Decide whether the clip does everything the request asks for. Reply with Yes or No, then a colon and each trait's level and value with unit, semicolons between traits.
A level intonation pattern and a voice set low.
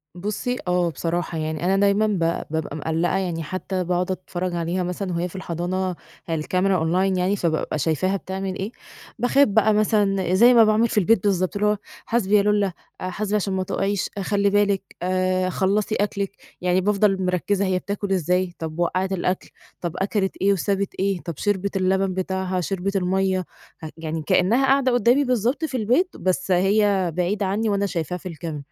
No: narrow, 2.2 semitones; high, 190 Hz